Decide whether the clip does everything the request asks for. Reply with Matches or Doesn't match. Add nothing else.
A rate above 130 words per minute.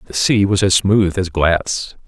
Matches